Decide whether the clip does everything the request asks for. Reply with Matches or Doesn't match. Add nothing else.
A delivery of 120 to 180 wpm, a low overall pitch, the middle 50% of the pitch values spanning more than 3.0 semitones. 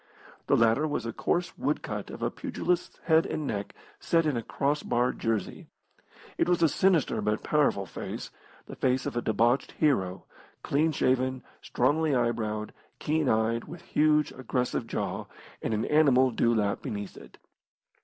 Matches